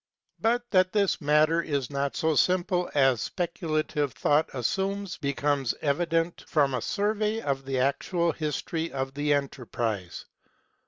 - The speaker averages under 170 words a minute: Yes, average, 140 wpm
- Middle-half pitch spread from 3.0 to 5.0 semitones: Yes, average, 4.3 semitones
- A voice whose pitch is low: No, medium, 150 Hz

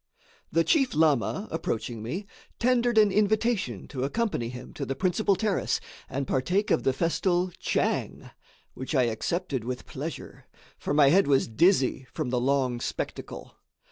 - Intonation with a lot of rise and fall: Yes, wide, 7.4 semitones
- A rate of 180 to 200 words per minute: No, average, 150 wpm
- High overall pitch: No, medium, 155 Hz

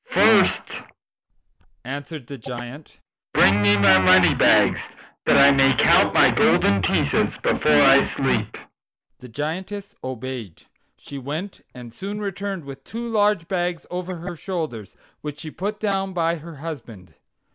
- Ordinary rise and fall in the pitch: No, wide, 7.1 semitones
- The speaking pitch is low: No, medium, 150 Hz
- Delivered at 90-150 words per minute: Yes, average, 140 wpm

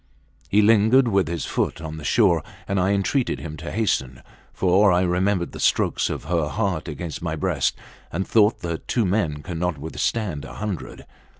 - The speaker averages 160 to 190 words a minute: Yes, average, 180 wpm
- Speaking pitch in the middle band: No, very low, 90 Hz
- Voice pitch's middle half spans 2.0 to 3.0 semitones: No, average, 4.2 semitones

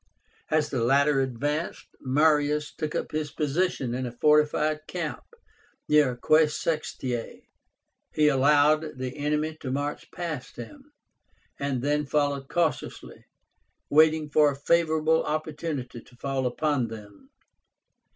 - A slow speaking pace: Yes, slow, 125 wpm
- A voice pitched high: No, medium, 150 Hz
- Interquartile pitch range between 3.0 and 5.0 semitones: No, narrow, 2.4 semitones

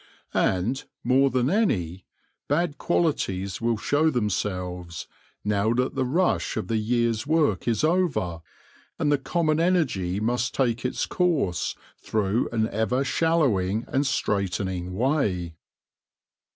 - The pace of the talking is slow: Yes, slow, 125 wpm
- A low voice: Yes, low, 120 Hz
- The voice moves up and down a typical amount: No, wide, 6.9 semitones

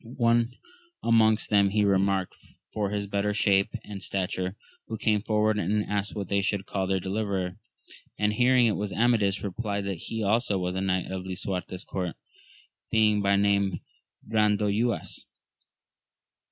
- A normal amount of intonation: No, narrow, 1.8 semitones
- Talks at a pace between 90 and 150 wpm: Yes, average, 145 wpm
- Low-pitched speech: Yes, low, 100 Hz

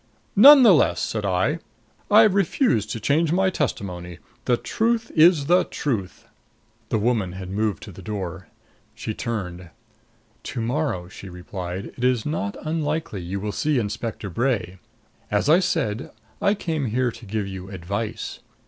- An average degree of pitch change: No, wide, 8.0 semitones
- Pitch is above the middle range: No, low, 115 Hz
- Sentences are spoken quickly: No, average, 155 wpm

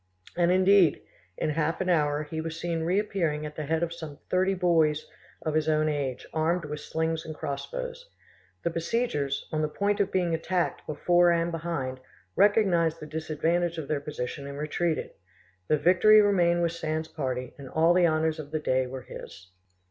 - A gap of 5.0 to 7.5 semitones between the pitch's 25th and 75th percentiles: No, narrow, 2.5 semitones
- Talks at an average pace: Yes, average, 180 wpm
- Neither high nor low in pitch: Yes, medium, 160 Hz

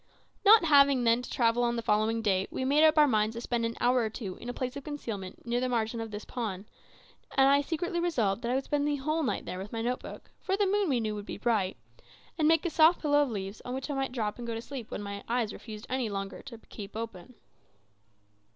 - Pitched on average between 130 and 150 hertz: No, high, 240 Hz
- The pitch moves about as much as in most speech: Yes, average, 4.5 semitones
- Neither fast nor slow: No, fast, 260 wpm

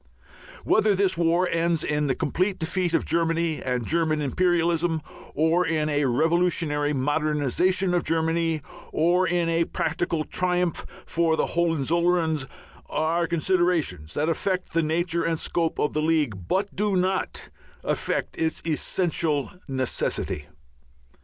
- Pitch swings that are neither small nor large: No, narrow, 2.3 semitones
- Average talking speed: No, slow, 130 wpm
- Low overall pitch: No, medium, 165 Hz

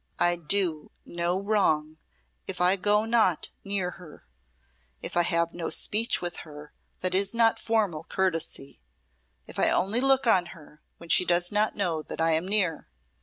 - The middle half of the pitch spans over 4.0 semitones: No, average, 3.6 semitones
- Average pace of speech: Yes, average, 170 wpm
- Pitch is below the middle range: No, medium, 180 Hz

